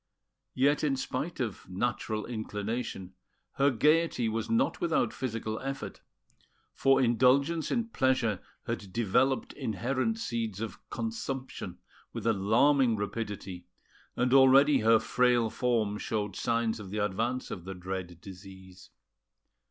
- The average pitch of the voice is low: Yes, low, 115 Hz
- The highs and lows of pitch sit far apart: No, average, 4.4 semitones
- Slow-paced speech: Yes, slow, 120 wpm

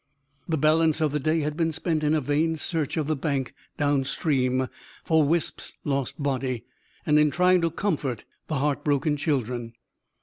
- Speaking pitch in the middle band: Yes, medium, 150 Hz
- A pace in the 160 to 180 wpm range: Yes, average, 170 wpm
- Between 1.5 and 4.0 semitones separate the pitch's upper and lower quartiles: Yes, narrow, 2.6 semitones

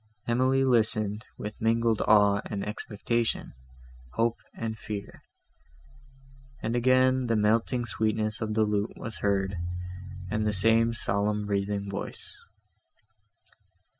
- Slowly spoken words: Yes, slow, 110 wpm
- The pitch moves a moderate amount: No, narrow, 2.0 semitones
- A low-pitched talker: Yes, low, 110 Hz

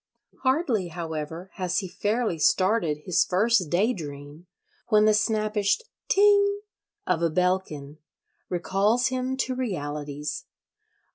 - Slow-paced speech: Yes, slow, 110 wpm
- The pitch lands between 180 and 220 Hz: Yes, high, 190 Hz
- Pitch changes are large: Yes, wide, 6.1 semitones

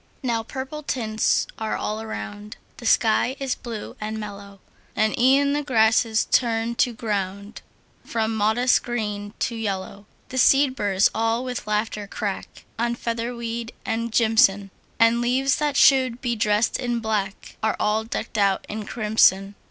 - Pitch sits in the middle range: No, high, 225 Hz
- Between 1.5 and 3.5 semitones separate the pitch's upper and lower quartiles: Yes, narrow, 2.4 semitones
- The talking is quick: No, average, 150 wpm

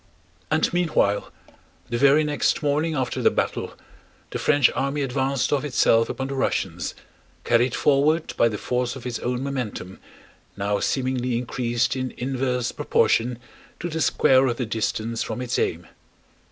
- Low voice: Yes, low, 125 Hz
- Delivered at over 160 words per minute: No, average, 155 wpm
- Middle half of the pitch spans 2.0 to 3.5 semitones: Yes, average, 2.8 semitones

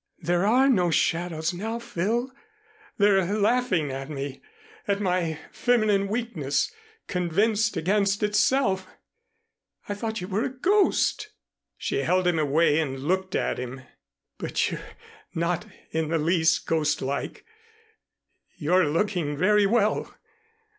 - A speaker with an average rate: No, slow, 120 wpm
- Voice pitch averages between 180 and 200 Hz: Yes, medium, 185 Hz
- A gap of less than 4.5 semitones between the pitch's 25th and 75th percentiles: No, average, 4.8 semitones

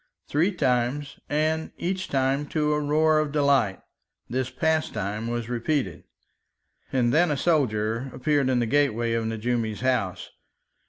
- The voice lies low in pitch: Yes, low, 130 Hz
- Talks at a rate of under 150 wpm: Yes, average, 140 wpm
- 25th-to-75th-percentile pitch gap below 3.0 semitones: No, average, 4.4 semitones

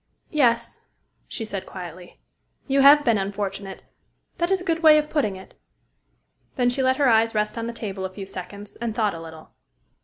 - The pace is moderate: Yes, average, 190 wpm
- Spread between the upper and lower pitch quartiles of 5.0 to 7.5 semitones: Yes, wide, 5.6 semitones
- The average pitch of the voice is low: No, high, 220 Hz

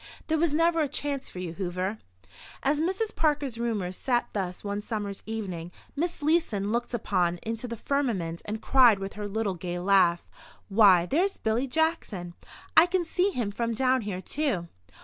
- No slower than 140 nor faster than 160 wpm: No, average, 170 wpm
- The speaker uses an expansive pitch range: Yes, wide, 7.0 semitones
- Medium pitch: No, high, 225 Hz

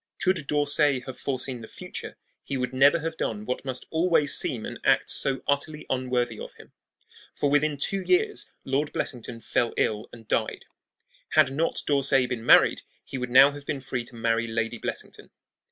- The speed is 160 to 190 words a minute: Yes, average, 180 wpm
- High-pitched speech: No, low, 135 Hz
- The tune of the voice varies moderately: Yes, average, 3.2 semitones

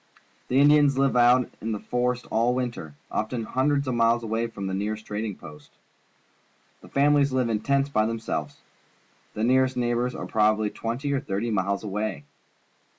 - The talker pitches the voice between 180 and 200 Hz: No, low, 120 Hz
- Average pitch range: Yes, average, 3.3 semitones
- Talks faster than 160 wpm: Yes, average, 170 wpm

